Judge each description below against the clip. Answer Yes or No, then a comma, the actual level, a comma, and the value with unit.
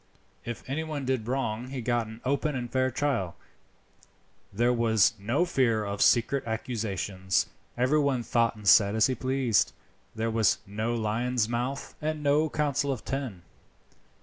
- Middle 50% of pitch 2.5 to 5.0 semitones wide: Yes, average, 3.5 semitones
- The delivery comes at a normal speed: Yes, average, 150 wpm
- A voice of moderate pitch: No, low, 120 Hz